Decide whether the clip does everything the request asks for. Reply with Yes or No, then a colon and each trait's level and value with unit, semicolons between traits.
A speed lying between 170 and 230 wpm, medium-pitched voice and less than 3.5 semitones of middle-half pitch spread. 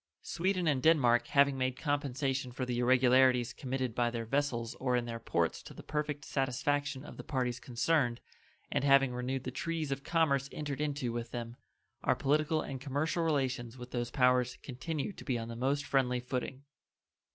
No: average, 180 wpm; low, 130 Hz; average, 2.7 semitones